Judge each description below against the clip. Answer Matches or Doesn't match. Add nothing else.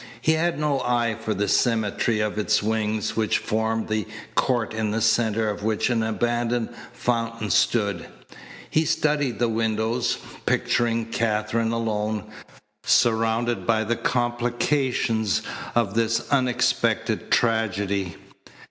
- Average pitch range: Doesn't match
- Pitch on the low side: Matches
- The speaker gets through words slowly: Matches